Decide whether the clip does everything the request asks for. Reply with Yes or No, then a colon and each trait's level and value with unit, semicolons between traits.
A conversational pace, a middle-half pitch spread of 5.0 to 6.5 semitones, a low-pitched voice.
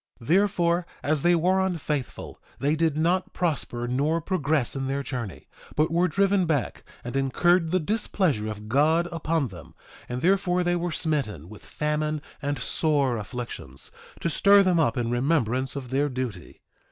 No: average, 165 wpm; average, 5.3 semitones; medium, 150 Hz